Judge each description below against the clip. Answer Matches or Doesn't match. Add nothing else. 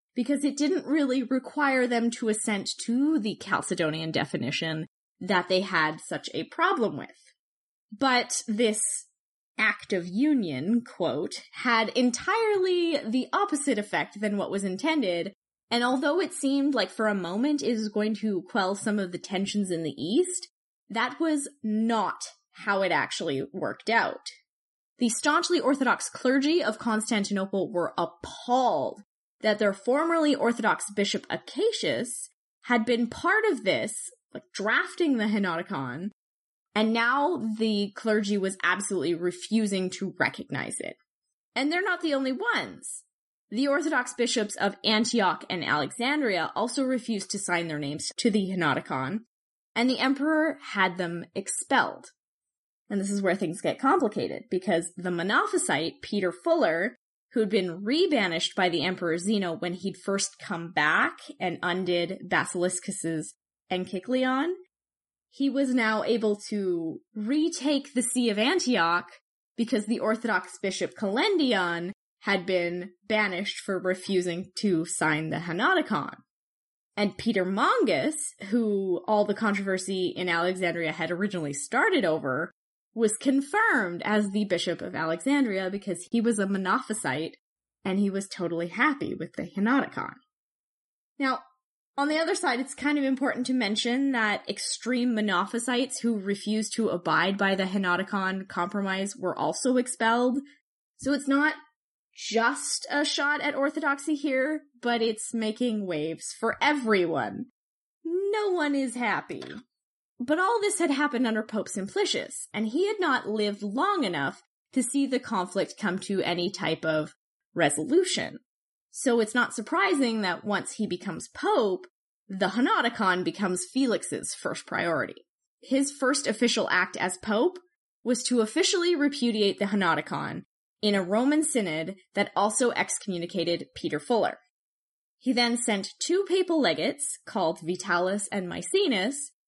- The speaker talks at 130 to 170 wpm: Matches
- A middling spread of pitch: Doesn't match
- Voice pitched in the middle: Doesn't match